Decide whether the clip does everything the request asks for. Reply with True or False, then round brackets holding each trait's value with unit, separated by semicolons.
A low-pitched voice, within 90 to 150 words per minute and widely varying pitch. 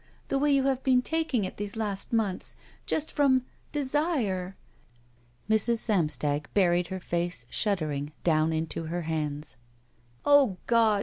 False (200 Hz; 140 wpm; 7.9 semitones)